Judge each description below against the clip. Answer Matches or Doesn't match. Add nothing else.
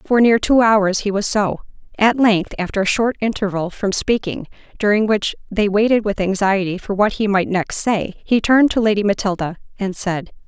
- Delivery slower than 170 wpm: Doesn't match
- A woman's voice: Matches